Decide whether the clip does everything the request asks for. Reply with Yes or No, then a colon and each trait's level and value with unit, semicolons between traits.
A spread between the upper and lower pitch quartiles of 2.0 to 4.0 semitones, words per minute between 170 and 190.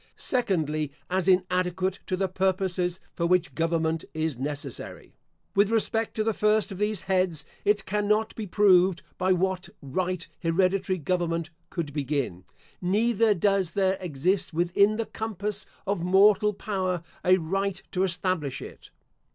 No: average, 2.9 semitones; average, 140 wpm